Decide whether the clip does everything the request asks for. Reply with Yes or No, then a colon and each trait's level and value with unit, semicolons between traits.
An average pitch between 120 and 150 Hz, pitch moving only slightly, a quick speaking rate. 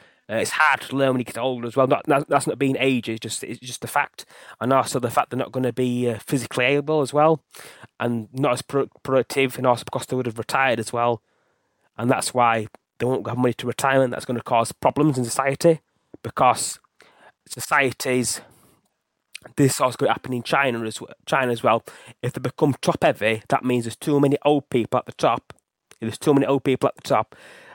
Yes: low, 130 Hz; narrow, 2.3 semitones; fast, 225 wpm